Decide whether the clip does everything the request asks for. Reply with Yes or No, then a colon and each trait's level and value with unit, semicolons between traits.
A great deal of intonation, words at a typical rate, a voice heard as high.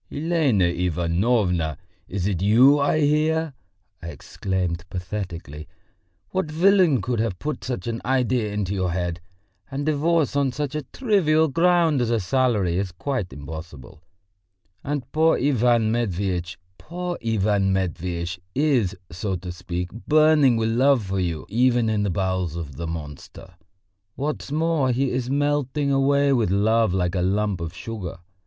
No: wide, 7.8 semitones; average, 150 wpm; low, 110 Hz